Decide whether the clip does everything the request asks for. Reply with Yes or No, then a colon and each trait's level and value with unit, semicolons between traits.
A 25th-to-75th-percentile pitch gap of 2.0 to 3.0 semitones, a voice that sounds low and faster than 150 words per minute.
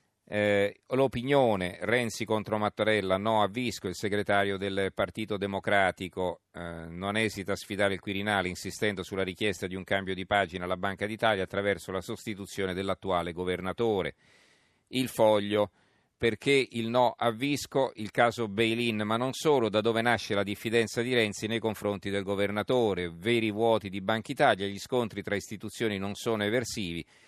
Yes: narrow, 2.6 semitones; low, 105 Hz; average, 160 wpm